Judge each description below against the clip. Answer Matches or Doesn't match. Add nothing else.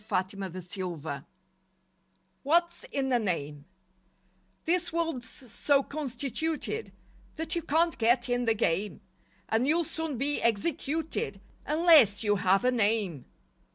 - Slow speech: Matches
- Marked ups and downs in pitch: Matches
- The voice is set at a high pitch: Matches